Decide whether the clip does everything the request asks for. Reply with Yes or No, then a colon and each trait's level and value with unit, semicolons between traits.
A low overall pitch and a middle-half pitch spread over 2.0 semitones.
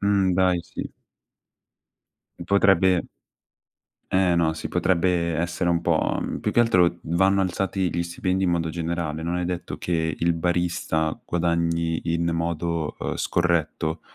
No: very low, 85 Hz; narrow, 1.6 semitones